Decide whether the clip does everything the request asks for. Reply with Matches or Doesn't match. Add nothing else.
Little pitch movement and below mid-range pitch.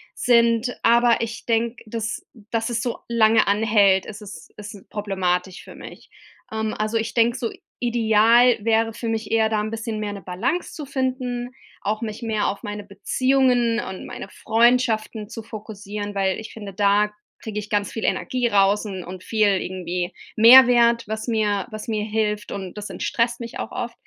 Doesn't match